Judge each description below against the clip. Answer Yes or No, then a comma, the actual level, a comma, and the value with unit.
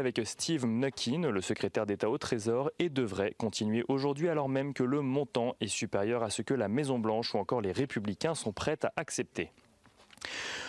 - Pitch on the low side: Yes, low, 125 Hz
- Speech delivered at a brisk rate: No, average, 185 wpm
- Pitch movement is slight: No, average, 3.4 semitones